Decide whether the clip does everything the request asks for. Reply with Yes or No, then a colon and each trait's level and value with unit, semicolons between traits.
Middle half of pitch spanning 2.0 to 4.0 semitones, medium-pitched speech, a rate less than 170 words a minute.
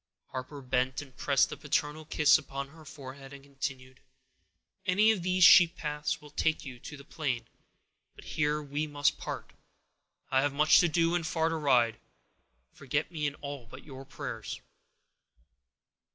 Yes: narrow, 2.5 semitones; medium, 145 Hz; average, 160 wpm